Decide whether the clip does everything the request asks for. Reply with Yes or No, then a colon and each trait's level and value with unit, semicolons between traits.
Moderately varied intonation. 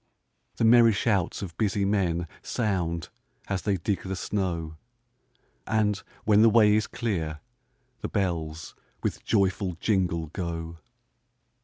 Yes: average, 3.9 semitones